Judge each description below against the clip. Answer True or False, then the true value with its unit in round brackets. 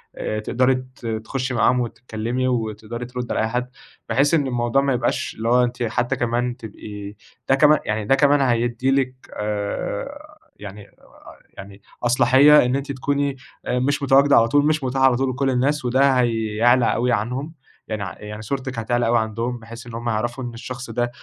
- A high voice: False (125 Hz)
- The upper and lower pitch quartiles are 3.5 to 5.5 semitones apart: False (2.7 semitones)